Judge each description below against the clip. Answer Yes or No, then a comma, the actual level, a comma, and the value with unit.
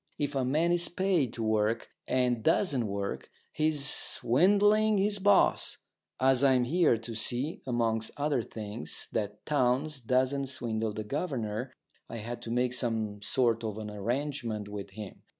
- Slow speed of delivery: No, average, 150 wpm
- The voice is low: Yes, low, 125 Hz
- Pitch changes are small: No, average, 4.9 semitones